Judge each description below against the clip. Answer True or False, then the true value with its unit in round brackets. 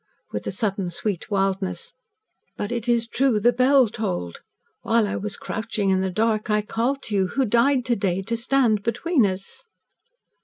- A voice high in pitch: True (220 Hz)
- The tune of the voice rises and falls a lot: False (3.6 semitones)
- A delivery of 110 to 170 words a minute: False (180 wpm)